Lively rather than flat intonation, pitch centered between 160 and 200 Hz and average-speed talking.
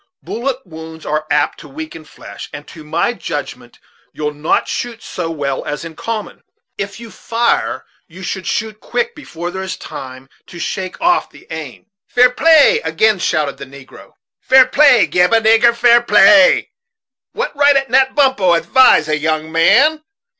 Yes: wide, 8.1 semitones; high, 190 Hz; average, 170 wpm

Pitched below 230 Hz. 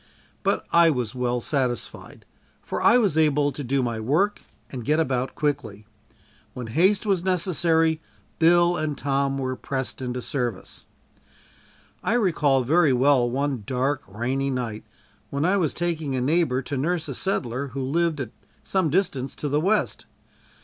Yes: medium, 140 Hz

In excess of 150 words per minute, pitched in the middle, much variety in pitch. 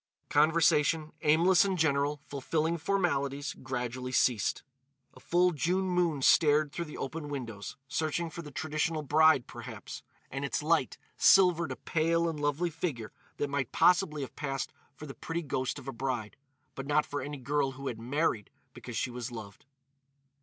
No: average, 160 wpm; medium, 145 Hz; average, 3.5 semitones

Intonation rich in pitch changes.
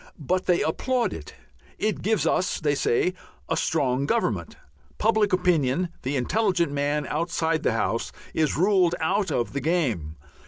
No: average, 4.8 semitones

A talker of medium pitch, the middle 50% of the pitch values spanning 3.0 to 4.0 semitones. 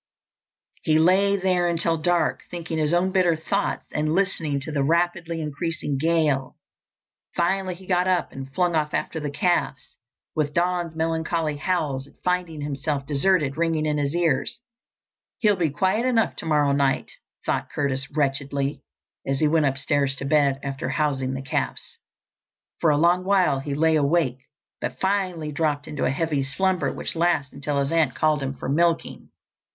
Yes: medium, 155 Hz; average, 3.6 semitones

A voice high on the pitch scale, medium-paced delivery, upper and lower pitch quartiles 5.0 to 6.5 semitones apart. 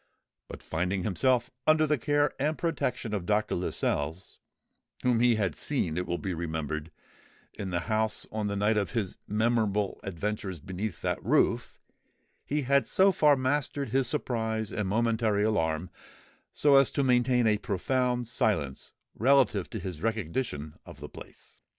No: low, 110 Hz; average, 150 wpm; average, 5.3 semitones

